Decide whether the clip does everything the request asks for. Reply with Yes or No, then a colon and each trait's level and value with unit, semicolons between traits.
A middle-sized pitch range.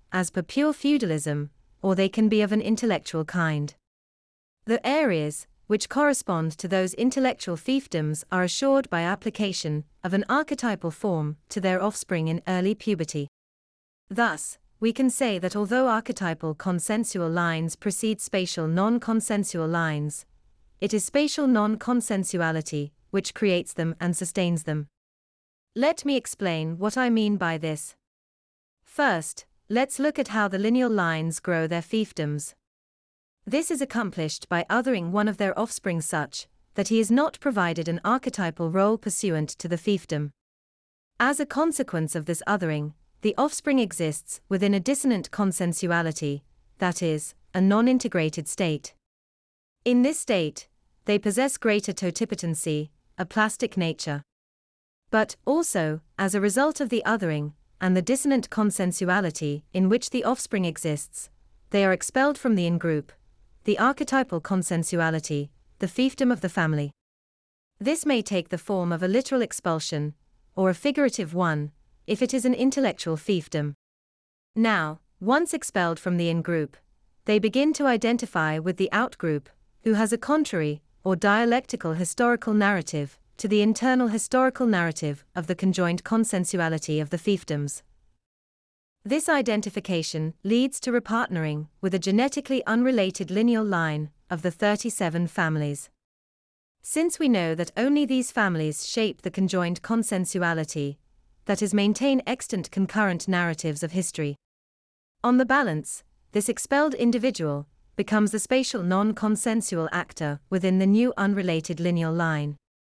No: wide, 6.1 semitones